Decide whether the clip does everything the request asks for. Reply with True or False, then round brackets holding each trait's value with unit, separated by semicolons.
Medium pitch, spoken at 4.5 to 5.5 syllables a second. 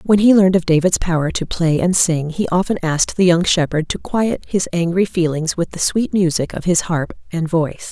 True (175 Hz; 5.3 syllables/s)